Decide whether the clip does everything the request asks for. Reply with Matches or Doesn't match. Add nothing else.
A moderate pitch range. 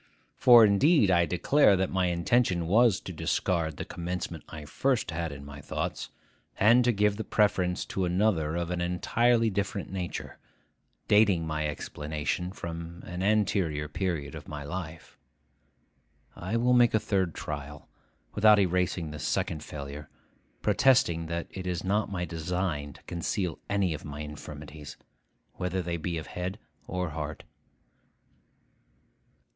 Matches